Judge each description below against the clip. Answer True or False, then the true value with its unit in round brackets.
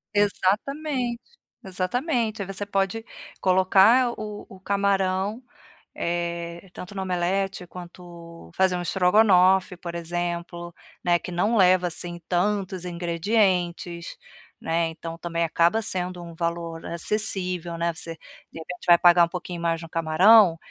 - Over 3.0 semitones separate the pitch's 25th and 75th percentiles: False (2.5 semitones)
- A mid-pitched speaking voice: True (180 Hz)